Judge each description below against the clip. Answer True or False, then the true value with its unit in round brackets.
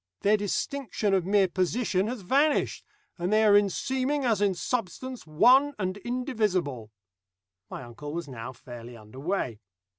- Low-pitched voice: False (200 Hz)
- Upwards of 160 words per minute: False (150 wpm)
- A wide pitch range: True (7.9 semitones)